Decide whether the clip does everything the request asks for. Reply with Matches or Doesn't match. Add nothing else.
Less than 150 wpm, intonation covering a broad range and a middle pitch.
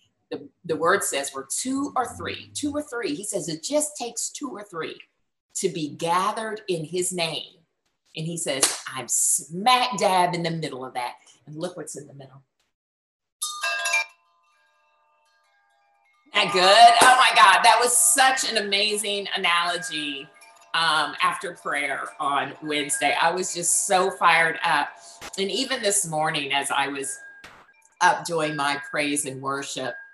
Doesn't match